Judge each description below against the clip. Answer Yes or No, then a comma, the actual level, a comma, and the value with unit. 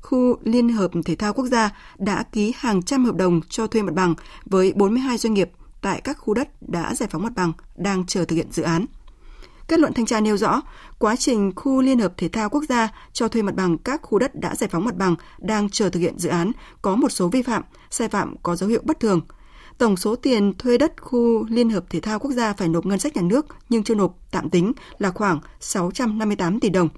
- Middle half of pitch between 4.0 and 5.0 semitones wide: Yes, average, 4.7 semitones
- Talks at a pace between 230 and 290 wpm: Yes, average, 240 wpm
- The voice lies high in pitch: Yes, high, 215 Hz